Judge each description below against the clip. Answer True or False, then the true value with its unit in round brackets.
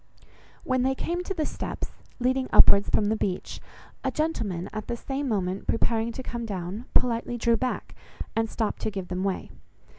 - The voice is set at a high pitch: True (230 Hz)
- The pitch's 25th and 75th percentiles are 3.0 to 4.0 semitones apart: False (4.4 semitones)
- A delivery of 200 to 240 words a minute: False (180 wpm)